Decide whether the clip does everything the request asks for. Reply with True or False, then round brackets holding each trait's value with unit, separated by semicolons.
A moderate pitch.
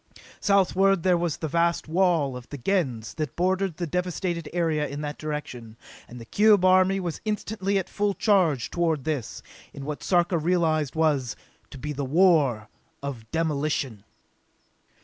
True (160 Hz)